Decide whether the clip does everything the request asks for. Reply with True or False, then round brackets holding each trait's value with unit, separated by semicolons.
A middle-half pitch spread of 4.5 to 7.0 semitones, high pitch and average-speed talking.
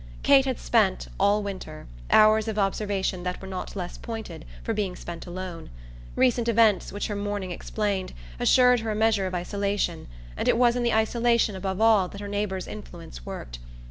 False (3.0 semitones; 205 Hz; 180 wpm)